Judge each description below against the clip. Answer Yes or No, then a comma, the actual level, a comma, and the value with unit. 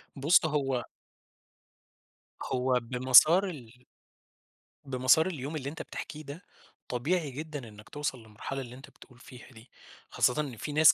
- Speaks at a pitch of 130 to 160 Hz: Yes, low, 135 Hz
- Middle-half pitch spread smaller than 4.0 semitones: Yes, average, 3.4 semitones